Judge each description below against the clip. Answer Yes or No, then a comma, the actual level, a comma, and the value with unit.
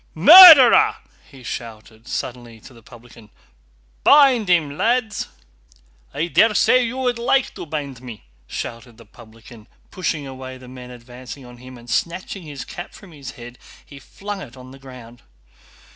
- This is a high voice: No, low, 130 Hz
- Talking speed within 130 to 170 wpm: Yes, average, 155 wpm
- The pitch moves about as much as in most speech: No, wide, 7.6 semitones